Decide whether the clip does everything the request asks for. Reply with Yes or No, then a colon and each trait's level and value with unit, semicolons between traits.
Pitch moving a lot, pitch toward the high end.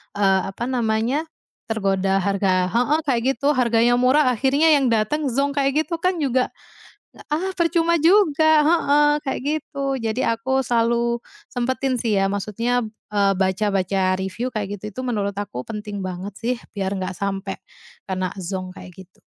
Yes: wide, 5.8 semitones; high, 235 Hz